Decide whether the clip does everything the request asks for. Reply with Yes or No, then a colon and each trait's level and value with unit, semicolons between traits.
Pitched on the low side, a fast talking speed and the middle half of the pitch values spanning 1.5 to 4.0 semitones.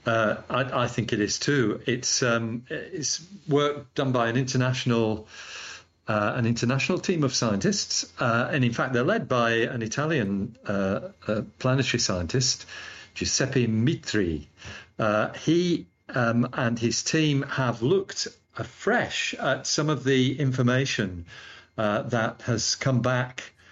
No: low, 125 Hz; average, 140 wpm; average, 3.1 semitones